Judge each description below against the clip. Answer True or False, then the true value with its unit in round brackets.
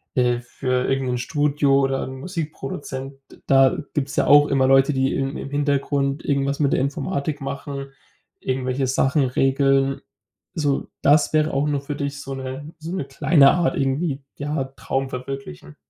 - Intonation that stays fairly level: True (1.3 semitones)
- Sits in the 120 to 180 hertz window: True (135 Hz)